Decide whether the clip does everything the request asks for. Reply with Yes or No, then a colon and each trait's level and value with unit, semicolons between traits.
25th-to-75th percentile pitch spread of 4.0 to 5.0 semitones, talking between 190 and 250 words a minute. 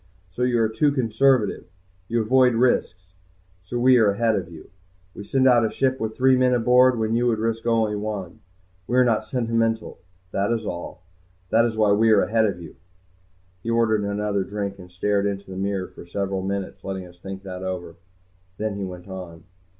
No: average, 3.3 semitones; average, 195 wpm